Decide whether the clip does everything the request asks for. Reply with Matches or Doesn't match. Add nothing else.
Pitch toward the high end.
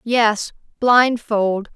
Matches